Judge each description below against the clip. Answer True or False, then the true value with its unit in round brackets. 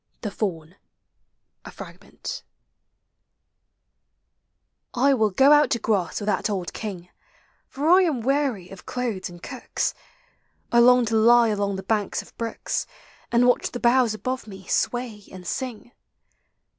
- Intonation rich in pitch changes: False (3.9 semitones)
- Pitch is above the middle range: True (230 Hz)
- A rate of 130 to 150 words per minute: True (145 wpm)